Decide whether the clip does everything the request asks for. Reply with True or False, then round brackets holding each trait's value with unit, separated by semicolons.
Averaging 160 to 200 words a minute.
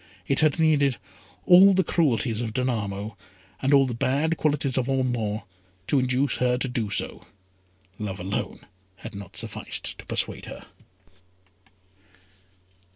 False (135 wpm)